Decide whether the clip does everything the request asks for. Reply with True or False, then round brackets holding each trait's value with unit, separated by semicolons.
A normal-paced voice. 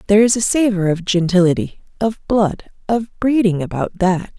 True (165 wpm)